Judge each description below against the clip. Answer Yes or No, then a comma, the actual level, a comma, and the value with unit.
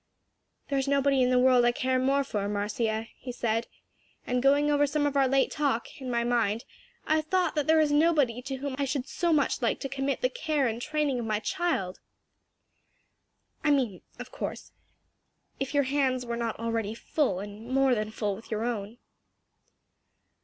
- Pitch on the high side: Yes, very high, 260 Hz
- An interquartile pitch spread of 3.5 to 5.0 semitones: Yes, average, 3.8 semitones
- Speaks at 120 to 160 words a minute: No, average, 185 wpm